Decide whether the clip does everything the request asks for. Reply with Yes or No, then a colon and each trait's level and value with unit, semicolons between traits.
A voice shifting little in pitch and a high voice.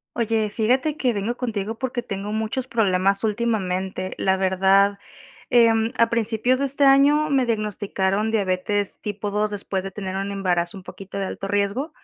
No: average, 3.2 semitones; high, 210 Hz